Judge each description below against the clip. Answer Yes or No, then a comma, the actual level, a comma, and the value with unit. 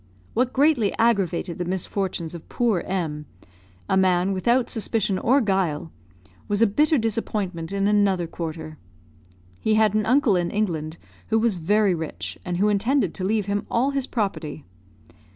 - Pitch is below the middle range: No, high, 200 Hz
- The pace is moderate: Yes, average, 155 wpm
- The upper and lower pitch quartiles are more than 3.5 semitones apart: Yes, average, 4.1 semitones